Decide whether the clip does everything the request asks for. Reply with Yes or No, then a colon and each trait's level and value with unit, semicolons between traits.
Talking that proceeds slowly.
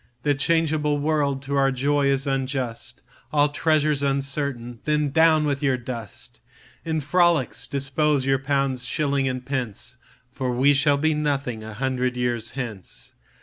Yes: slow, 130 wpm